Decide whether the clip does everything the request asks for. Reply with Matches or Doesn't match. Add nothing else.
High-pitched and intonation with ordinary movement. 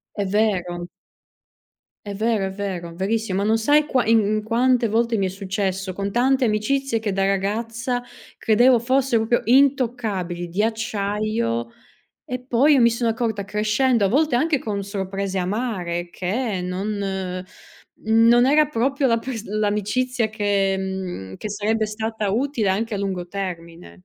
Matches